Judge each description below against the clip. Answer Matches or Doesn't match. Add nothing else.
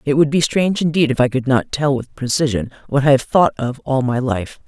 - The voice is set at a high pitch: Doesn't match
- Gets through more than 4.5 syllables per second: Matches